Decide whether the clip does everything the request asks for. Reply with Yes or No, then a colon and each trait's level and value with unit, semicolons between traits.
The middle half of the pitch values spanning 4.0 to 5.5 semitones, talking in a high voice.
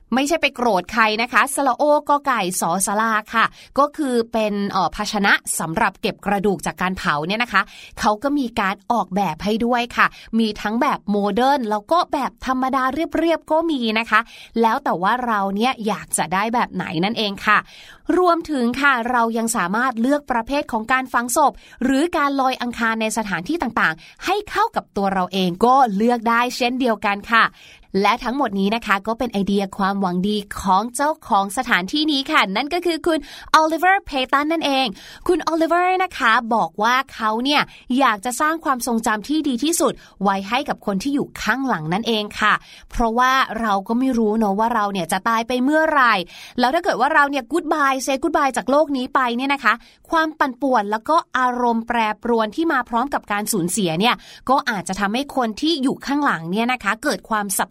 Yes: average, 5.1 semitones; high, 235 Hz